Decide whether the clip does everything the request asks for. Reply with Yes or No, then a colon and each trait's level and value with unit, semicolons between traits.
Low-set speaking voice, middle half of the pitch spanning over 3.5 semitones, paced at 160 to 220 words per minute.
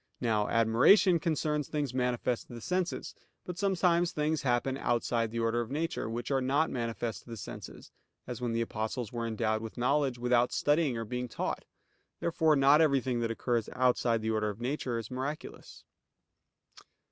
Yes: low, 125 Hz; average, 4.4 semitones; average, 170 wpm